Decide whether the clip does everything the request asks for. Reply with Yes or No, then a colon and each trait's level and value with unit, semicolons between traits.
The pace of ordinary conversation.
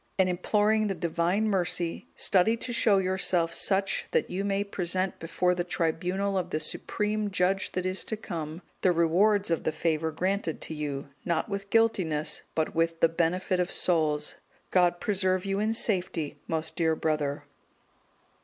Yes: average, 165 wpm